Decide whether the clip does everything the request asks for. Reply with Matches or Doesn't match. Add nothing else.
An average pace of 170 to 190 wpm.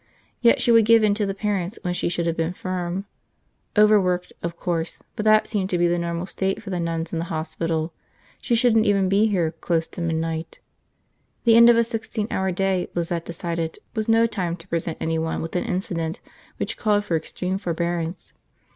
Doesn't match